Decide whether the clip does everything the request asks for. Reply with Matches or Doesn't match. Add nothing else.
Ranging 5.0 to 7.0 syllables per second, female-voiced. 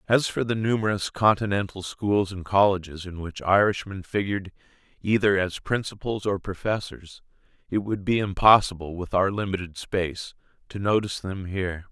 Doesn't match